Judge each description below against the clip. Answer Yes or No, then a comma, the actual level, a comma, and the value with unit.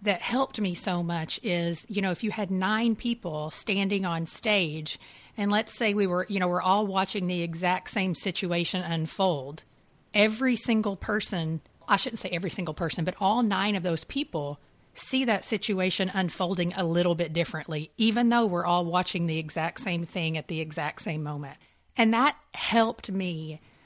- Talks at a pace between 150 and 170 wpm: No, average, 180 wpm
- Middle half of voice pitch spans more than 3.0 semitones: Yes, average, 4.0 semitones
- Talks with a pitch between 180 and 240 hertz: Yes, medium, 185 Hz